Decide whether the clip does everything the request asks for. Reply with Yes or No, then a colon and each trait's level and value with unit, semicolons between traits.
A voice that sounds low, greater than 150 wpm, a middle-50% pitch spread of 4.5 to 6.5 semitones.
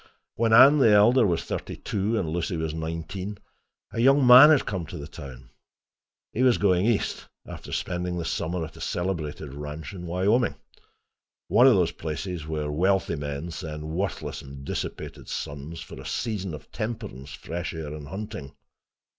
Yes: very low, 85 Hz; average, 165 wpm; average, 5.2 semitones